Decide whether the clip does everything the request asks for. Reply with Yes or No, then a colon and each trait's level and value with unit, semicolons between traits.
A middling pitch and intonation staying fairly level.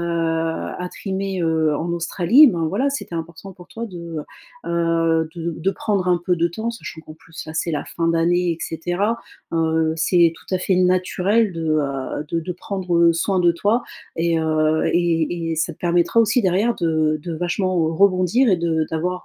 Yes: medium, 170 Hz; narrow, 2.2 semitones